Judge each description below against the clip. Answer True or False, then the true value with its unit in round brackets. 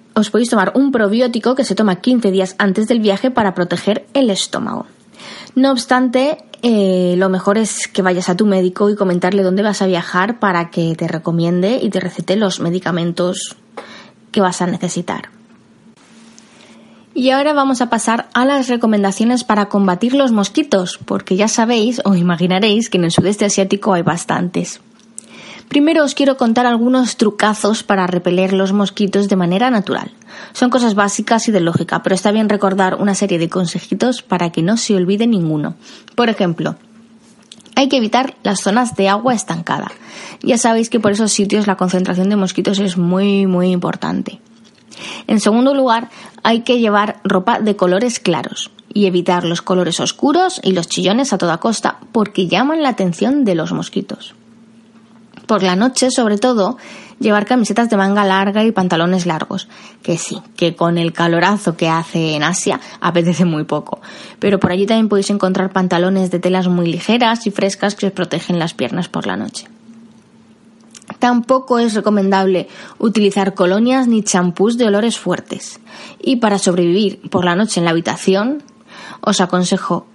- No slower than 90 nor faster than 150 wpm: False (170 wpm)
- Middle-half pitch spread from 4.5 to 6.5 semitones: False (3.8 semitones)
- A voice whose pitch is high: True (205 Hz)